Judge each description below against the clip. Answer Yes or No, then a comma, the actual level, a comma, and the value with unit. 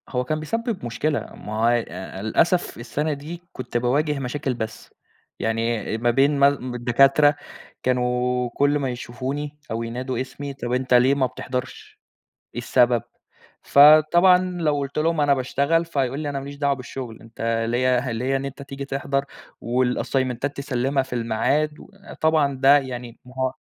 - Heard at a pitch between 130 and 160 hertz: Yes, low, 135 Hz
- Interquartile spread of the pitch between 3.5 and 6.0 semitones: No, average, 2.7 semitones